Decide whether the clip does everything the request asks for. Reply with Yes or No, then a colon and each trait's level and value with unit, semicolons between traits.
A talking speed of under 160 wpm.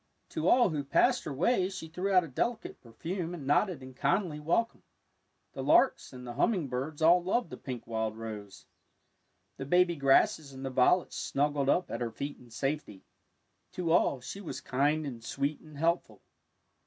No: average, 180 wpm